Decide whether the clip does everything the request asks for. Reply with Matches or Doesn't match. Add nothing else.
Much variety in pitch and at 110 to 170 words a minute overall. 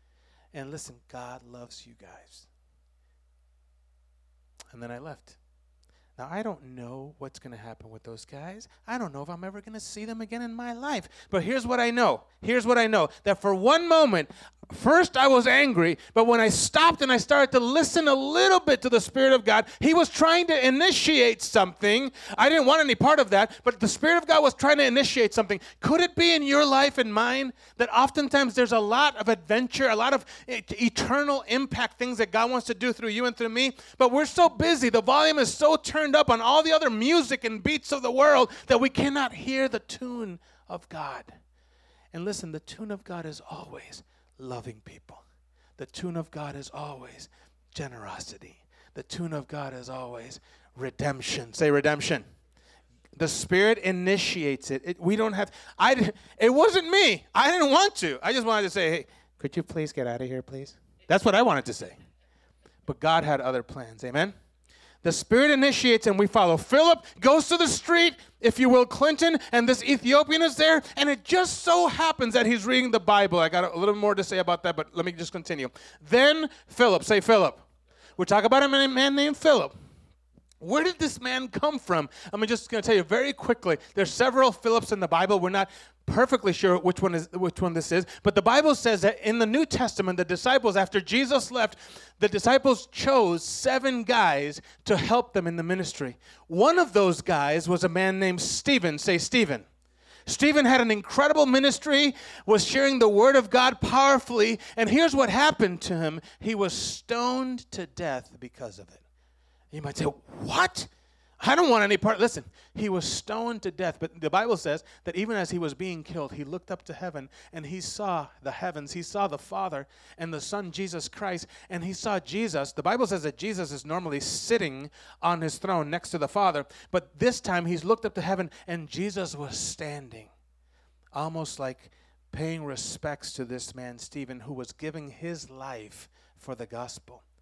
Doesn't match